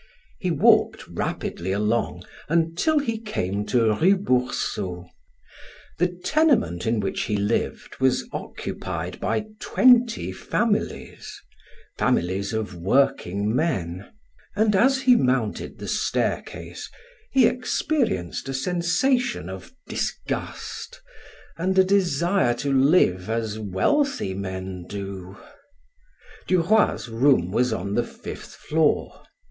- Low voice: Yes, low, 125 Hz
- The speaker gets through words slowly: Yes, slow, 105 wpm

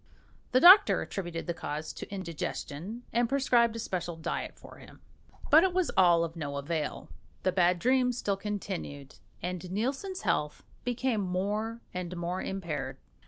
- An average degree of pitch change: No, wide, 5.8 semitones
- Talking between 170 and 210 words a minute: No, average, 155 wpm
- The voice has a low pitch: No, high, 190 Hz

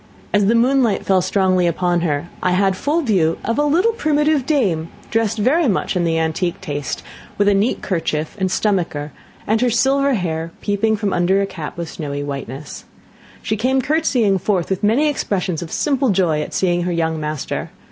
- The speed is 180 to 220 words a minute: Yes, average, 190 wpm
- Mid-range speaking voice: No, high, 195 Hz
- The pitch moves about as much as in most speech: No, wide, 5.9 semitones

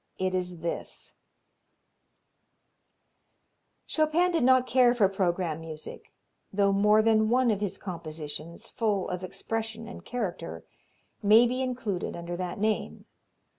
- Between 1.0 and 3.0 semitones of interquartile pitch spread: No, average, 4.8 semitones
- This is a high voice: Yes, high, 205 Hz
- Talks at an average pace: No, slow, 125 wpm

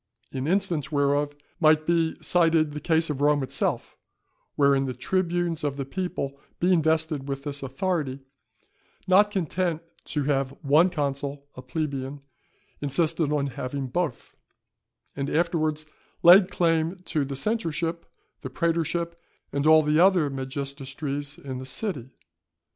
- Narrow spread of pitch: No, average, 3.4 semitones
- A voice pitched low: No, medium, 150 Hz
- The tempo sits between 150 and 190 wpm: No, slow, 135 wpm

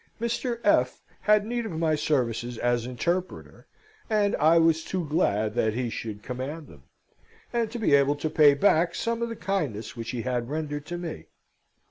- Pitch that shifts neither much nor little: No, wide, 7.2 semitones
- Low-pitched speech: No, medium, 155 Hz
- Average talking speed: Yes, average, 180 wpm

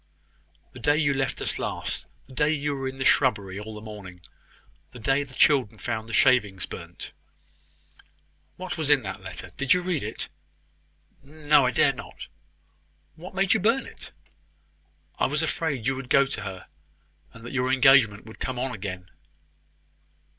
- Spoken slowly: No, average, 170 wpm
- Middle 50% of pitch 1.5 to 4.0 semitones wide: No, average, 4.9 semitones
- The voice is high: No, low, 130 Hz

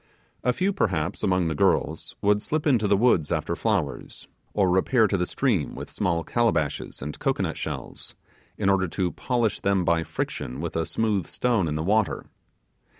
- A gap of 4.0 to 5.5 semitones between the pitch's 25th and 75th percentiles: Yes, average, 5.2 semitones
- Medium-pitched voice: No, very low, 95 Hz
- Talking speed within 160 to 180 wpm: Yes, average, 175 wpm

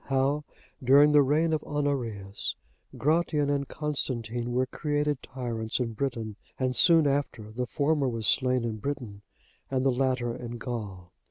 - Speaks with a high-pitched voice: No, low, 130 Hz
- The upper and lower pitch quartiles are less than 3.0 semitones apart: No, average, 3.7 semitones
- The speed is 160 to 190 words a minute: No, average, 150 wpm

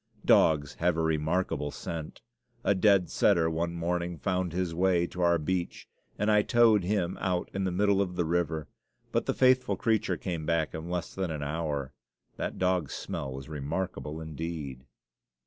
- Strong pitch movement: No, average, 2.8 semitones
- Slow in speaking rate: No, average, 170 wpm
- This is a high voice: No, very low, 85 Hz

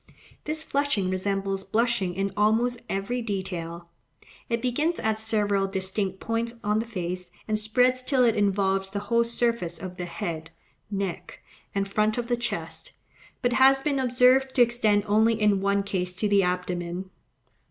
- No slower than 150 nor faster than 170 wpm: Yes, average, 160 wpm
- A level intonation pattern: No, average, 3.7 semitones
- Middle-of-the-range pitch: No, high, 210 Hz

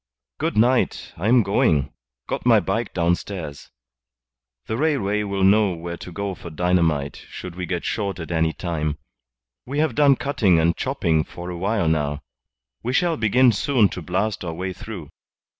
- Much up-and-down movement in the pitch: No, average, 4.7 semitones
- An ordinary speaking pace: Yes, average, 170 wpm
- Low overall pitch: Yes, very low, 95 Hz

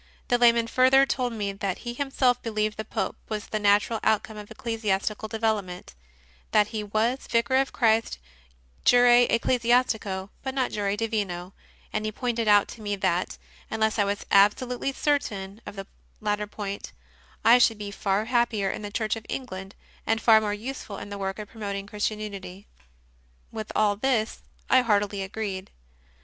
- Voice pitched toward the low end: No, high, 215 Hz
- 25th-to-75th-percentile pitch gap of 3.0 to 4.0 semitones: No, narrow, 2.6 semitones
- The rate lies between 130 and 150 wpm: No, average, 170 wpm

